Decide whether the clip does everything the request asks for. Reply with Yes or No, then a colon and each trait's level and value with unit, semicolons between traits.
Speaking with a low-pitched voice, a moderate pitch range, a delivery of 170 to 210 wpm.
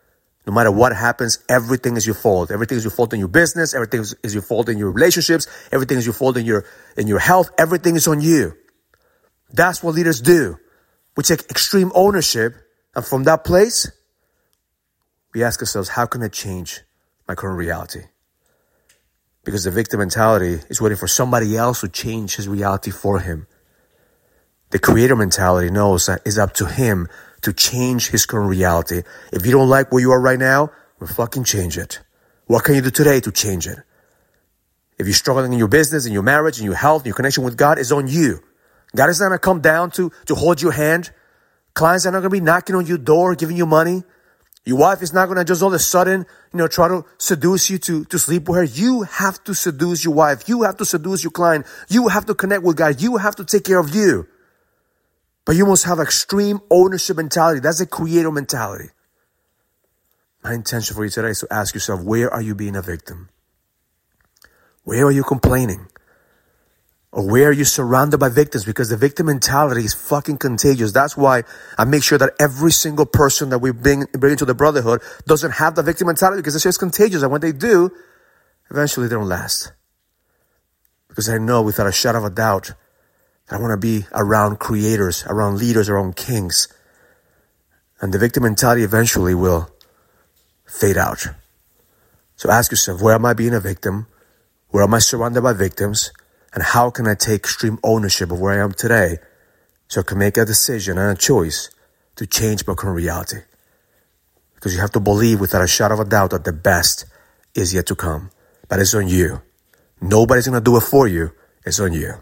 No: low, 120 Hz; wide, 7.7 semitones; average, 200 wpm